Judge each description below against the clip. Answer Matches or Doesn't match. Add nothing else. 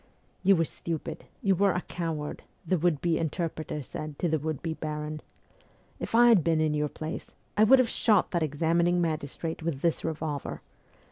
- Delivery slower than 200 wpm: Doesn't match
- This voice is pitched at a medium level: Matches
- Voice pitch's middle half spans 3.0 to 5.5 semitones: Doesn't match